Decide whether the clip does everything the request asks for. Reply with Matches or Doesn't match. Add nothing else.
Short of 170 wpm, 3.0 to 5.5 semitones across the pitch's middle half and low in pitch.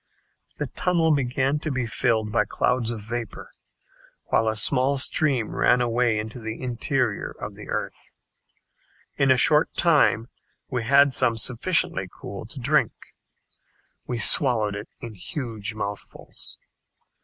Matches